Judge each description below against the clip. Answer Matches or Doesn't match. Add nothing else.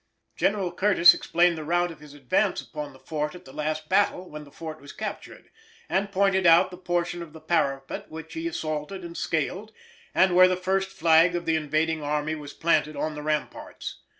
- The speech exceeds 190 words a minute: Matches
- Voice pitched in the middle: Matches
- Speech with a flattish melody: Doesn't match